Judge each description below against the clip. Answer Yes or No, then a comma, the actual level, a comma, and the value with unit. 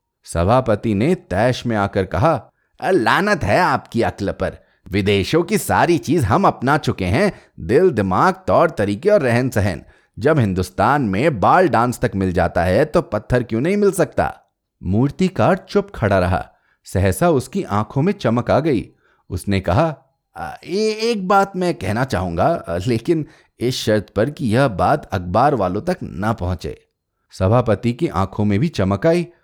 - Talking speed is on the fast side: No, average, 165 wpm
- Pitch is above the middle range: No, low, 120 Hz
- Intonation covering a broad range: Yes, wide, 8.7 semitones